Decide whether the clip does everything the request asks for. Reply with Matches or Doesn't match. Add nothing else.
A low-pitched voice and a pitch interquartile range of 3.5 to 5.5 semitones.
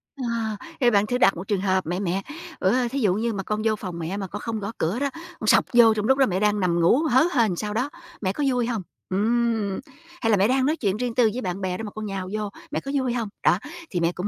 Doesn't match